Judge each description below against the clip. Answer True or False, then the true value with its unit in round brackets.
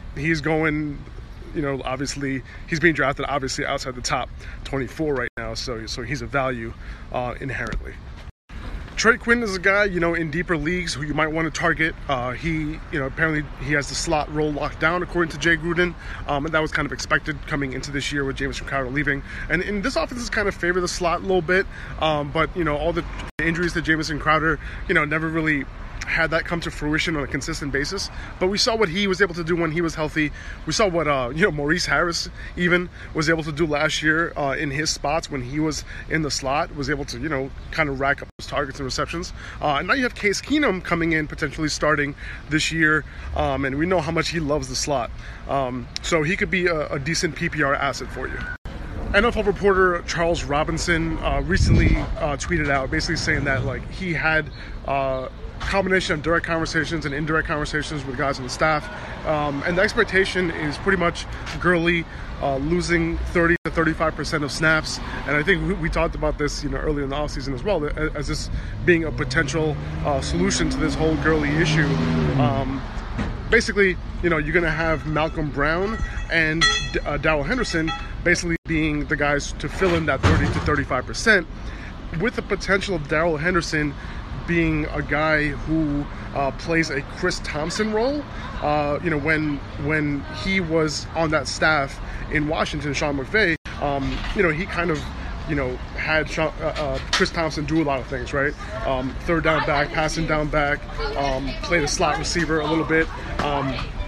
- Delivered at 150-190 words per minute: False (205 wpm)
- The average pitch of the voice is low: False (155 Hz)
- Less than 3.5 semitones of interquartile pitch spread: True (3.1 semitones)